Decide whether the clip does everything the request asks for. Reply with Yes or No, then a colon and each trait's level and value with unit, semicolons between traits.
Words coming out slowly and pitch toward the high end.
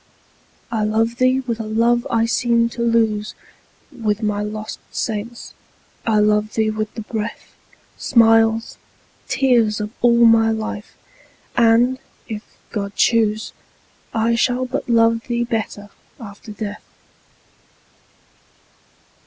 Yes: slow, 120 wpm; high, 225 Hz